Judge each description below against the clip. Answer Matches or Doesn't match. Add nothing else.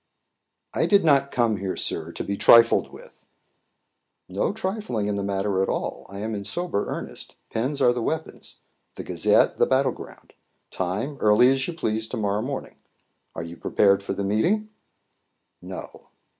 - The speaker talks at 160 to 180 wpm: Matches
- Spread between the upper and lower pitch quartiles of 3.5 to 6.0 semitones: Matches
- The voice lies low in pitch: Matches